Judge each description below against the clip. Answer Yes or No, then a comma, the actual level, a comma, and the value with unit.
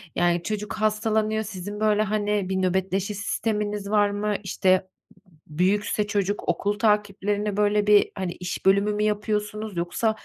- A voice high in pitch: Yes, high, 205 Hz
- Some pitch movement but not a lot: No, narrow, 1.5 semitones